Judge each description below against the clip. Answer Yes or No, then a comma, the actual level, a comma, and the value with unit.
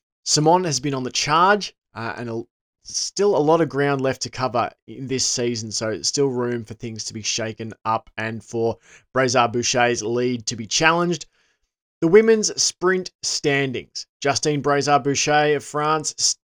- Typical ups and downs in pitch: Yes, average, 4.6 semitones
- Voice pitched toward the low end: Yes, low, 130 Hz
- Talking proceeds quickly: No, average, 170 wpm